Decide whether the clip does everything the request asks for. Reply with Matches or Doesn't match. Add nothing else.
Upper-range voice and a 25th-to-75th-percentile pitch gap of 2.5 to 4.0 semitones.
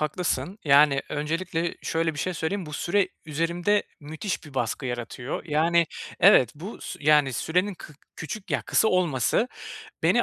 Doesn't match